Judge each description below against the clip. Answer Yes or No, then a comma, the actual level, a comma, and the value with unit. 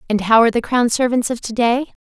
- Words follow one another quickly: Yes, fast, 265 wpm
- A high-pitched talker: Yes, high, 235 Hz